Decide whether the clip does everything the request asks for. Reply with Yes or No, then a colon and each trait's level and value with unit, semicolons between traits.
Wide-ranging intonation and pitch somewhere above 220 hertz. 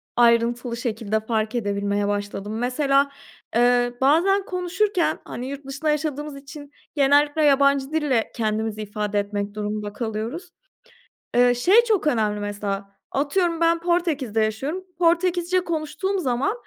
Yes: wide, 6.7 semitones; very high, 265 Hz